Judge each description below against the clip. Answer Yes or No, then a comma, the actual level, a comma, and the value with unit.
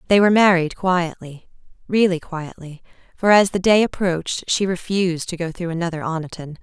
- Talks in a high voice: No, medium, 175 Hz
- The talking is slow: No, average, 155 wpm